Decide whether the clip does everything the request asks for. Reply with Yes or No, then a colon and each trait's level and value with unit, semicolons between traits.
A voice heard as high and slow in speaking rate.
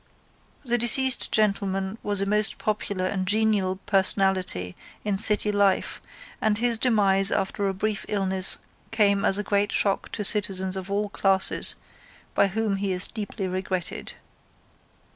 No: high, 200 Hz; average, 145 wpm